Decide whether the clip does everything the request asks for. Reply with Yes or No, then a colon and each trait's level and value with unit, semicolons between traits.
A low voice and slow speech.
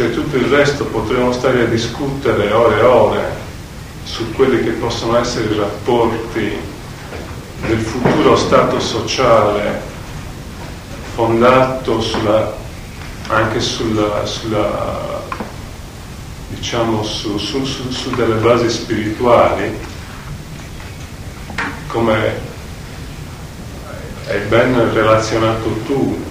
Yes: low, 115 Hz; slow, 90 wpm